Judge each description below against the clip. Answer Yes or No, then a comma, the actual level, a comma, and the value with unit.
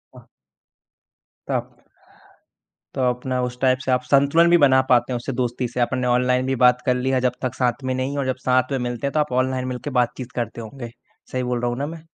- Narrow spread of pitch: Yes, narrow, 1.2 semitones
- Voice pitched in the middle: No, low, 130 Hz